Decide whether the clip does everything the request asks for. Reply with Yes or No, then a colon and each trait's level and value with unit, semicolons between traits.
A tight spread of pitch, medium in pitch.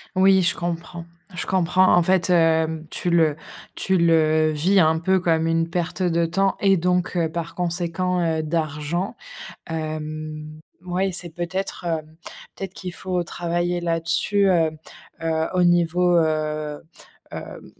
Yes: narrow, 2.1 semitones; medium, 170 Hz